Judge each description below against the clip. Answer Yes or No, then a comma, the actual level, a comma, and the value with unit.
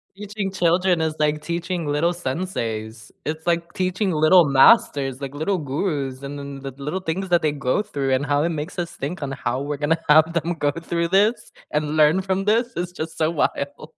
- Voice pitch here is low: No, medium, 160 Hz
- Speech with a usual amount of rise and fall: Yes, average, 3.8 semitones